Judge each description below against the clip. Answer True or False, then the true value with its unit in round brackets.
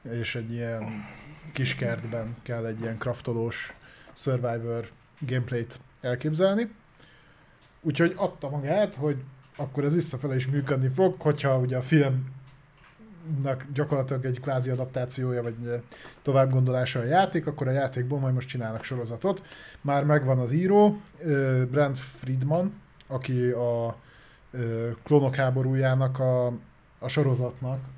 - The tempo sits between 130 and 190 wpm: False (120 wpm)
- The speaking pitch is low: True (130 Hz)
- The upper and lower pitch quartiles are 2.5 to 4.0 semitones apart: True (3.0 semitones)